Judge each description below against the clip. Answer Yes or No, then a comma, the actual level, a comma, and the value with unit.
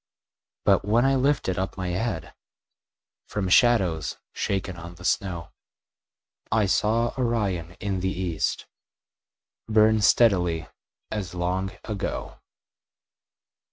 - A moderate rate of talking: No, slow, 105 wpm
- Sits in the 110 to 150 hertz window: No, very low, 95 Hz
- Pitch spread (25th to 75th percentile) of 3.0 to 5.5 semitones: Yes, average, 3.8 semitones